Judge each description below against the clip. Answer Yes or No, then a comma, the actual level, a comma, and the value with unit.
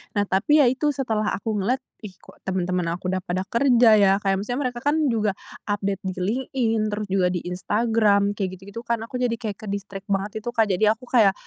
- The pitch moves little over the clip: No, average, 3.3 semitones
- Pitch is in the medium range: No, high, 210 Hz